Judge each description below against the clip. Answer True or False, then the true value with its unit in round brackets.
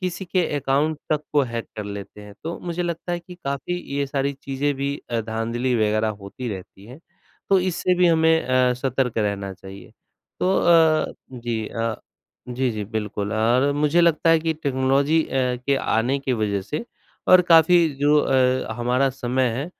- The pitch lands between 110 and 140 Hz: True (135 Hz)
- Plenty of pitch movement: True (6.0 semitones)